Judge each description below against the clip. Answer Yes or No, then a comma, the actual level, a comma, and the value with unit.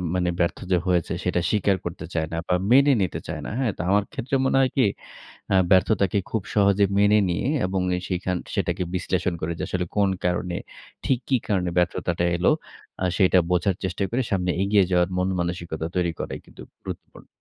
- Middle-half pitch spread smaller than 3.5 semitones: Yes, narrow, 2.4 semitones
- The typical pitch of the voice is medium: No, very low, 90 Hz